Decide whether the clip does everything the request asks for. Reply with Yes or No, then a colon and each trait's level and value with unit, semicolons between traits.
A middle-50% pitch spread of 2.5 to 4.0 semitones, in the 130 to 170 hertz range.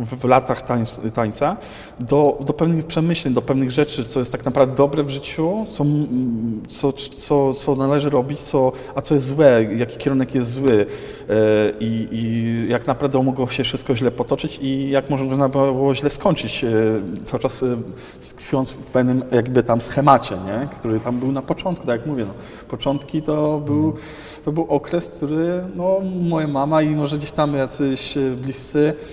Yes: average, 2.9 semitones; low, 135 Hz